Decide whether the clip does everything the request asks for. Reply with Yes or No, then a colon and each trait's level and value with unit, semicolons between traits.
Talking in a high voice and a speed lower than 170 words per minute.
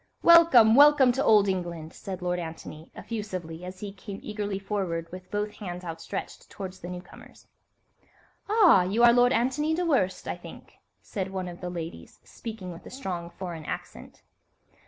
Yes: high, 195 Hz; average, 160 wpm